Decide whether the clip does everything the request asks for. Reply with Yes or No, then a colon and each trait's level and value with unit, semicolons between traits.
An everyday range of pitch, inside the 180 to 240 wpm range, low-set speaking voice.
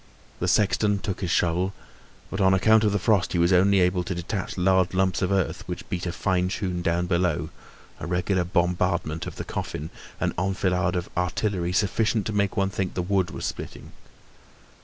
No: narrow, 1.8 semitones; average, 190 wpm; very low, 90 Hz